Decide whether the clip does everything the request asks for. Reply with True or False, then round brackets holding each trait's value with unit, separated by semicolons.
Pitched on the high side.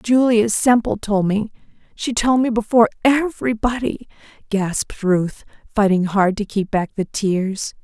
True (215 Hz)